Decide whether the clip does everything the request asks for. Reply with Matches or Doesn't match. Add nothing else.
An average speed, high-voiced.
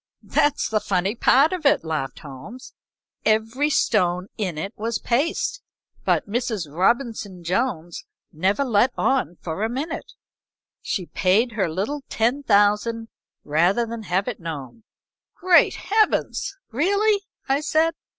Doesn't match